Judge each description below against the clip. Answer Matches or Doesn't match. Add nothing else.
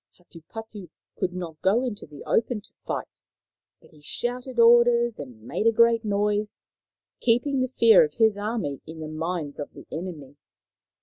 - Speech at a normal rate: Matches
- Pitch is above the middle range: Matches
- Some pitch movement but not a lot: Doesn't match